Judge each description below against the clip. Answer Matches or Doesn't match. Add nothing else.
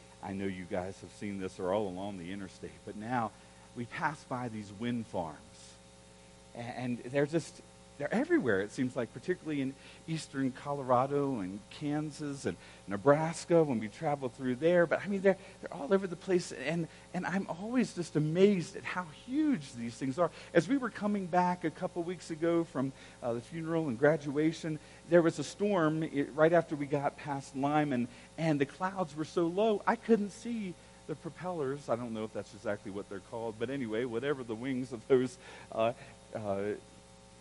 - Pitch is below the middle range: Doesn't match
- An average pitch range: Doesn't match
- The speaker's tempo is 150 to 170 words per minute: Doesn't match